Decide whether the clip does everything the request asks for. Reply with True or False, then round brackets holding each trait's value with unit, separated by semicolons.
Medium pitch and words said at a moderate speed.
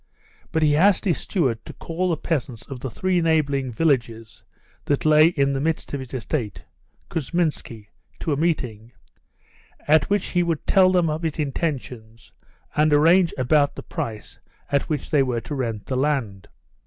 True (145 Hz; 170 wpm)